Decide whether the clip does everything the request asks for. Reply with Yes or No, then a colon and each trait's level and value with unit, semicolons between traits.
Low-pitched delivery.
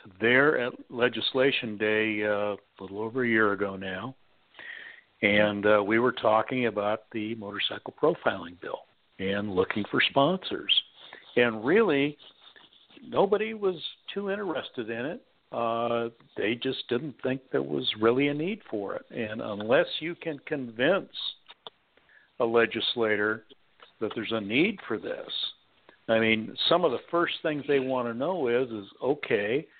Yes: low, 115 Hz